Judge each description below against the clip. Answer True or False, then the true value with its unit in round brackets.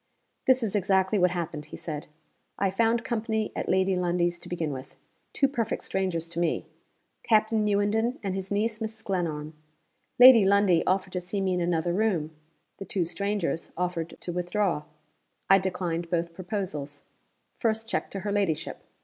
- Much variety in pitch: False (3.5 semitones)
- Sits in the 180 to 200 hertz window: True (190 Hz)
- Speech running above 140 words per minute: True (165 wpm)